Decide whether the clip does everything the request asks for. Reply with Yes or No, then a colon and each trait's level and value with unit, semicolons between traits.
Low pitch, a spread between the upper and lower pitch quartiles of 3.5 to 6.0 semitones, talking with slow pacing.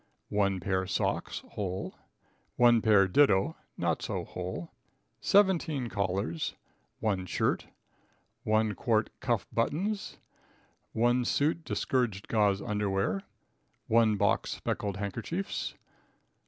Yes: low, 105 Hz; average, 3.9 semitones; slow, 100 wpm